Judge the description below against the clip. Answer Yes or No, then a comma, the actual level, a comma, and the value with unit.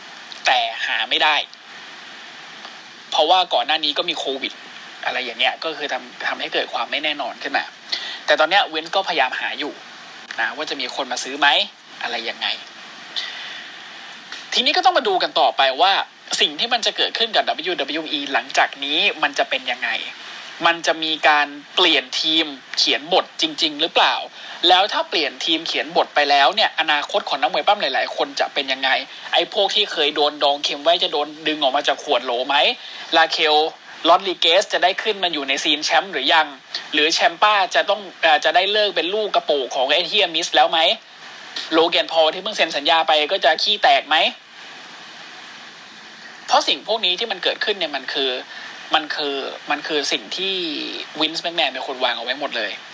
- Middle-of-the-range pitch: Yes, medium, 180 Hz